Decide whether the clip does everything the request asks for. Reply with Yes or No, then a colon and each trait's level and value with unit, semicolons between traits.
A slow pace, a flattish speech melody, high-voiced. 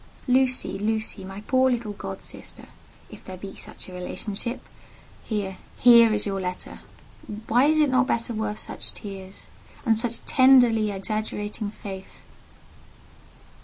No: slow, 130 wpm; average, 3.7 semitones; high, 215 Hz